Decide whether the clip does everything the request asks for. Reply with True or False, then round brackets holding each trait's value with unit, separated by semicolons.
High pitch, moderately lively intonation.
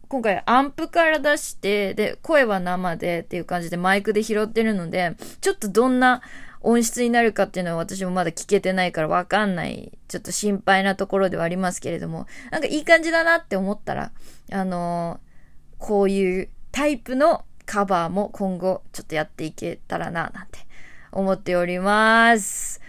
True (195 Hz; 4.1 semitones)